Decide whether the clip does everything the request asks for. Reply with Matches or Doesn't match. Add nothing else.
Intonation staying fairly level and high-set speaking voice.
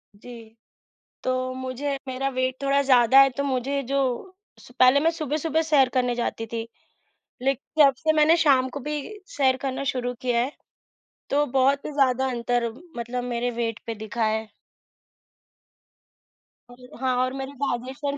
Matches